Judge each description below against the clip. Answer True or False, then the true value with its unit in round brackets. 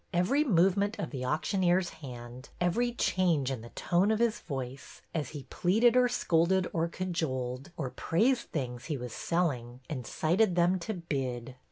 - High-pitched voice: False (170 Hz)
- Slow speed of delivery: False (165 wpm)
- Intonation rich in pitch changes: True (6.2 semitones)